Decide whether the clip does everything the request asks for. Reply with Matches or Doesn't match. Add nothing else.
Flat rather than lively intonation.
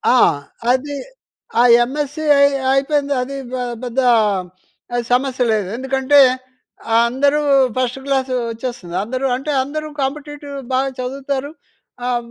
Matches